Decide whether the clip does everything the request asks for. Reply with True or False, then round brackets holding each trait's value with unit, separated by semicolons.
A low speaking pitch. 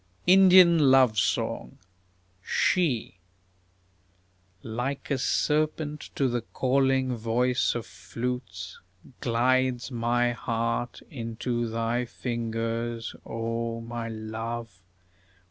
True (120 Hz)